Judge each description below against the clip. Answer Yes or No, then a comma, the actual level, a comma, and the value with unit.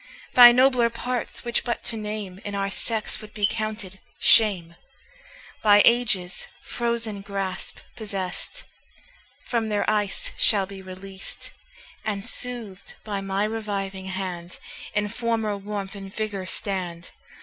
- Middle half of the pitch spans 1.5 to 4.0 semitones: Yes, narrow, 2.6 semitones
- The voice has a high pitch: Yes, high, 205 Hz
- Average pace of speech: No, slow, 125 wpm